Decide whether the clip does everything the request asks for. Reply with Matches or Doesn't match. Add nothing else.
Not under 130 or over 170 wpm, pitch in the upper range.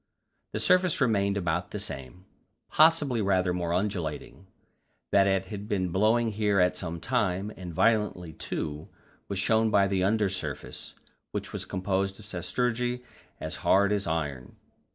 Doesn't match